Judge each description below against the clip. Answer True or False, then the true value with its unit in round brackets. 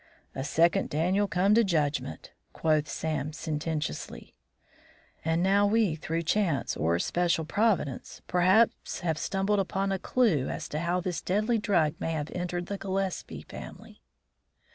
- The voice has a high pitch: False (175 Hz)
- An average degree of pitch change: True (3.9 semitones)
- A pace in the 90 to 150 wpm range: True (140 wpm)